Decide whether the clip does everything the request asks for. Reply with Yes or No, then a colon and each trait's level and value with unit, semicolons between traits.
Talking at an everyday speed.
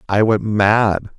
Yes: average, 150 wpm